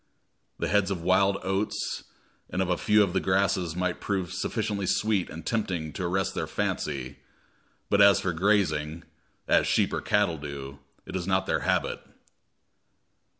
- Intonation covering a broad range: No, average, 2.9 semitones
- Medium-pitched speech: No, very low, 95 Hz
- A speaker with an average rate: Yes, average, 160 wpm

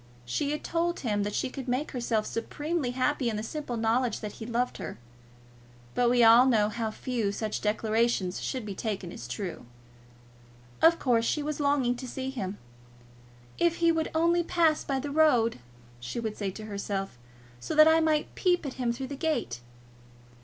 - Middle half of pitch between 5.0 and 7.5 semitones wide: Yes, wide, 5.5 semitones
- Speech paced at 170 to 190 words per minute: Yes, average, 185 wpm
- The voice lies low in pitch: No, high, 245 Hz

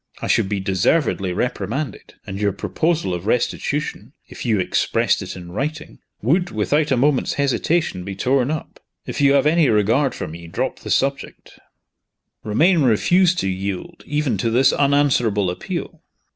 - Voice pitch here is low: Yes, low, 125 Hz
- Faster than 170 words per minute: No, average, 160 wpm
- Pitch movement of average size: No, wide, 6.9 semitones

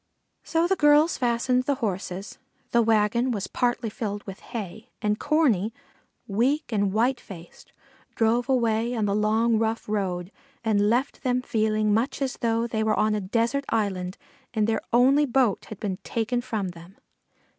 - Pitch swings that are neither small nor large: Yes, average, 3.0 semitones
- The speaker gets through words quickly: No, average, 165 wpm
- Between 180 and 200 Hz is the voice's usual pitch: No, high, 225 Hz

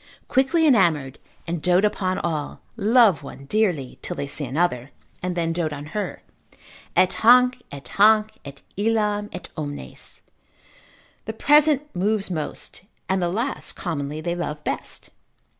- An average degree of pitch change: No, wide, 6.5 semitones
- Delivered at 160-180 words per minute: No, average, 140 wpm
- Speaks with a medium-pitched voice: Yes, medium, 180 Hz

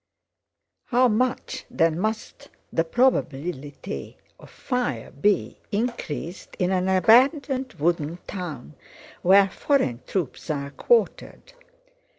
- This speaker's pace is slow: Yes, slow, 100 wpm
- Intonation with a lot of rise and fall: Yes, wide, 7.9 semitones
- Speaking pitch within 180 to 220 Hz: Yes, high, 190 Hz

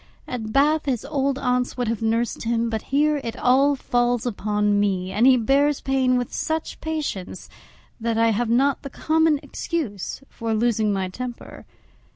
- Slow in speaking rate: No, average, 170 wpm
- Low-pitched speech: No, high, 245 Hz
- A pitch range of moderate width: Yes, average, 3.8 semitones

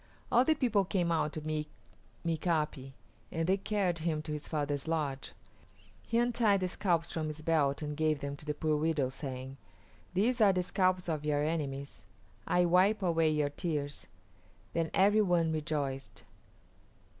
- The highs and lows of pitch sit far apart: No, average, 3.5 semitones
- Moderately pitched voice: Yes, medium, 160 Hz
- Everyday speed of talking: Yes, average, 165 wpm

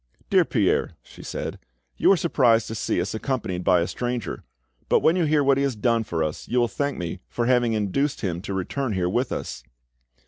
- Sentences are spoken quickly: Yes, fast, 215 wpm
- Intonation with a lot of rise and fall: Yes, wide, 6.4 semitones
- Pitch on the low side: Yes, low, 115 Hz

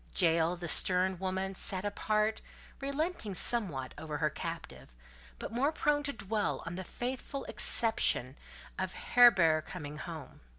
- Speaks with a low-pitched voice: No, high, 190 Hz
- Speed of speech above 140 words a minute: No, slow, 135 wpm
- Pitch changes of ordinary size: No, wide, 6.3 semitones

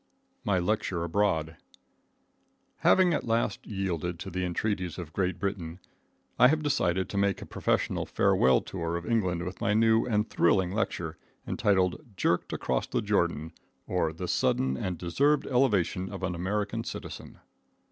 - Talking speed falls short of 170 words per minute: Yes, average, 150 wpm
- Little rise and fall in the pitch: No, average, 3.6 semitones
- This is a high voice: No, very low, 95 Hz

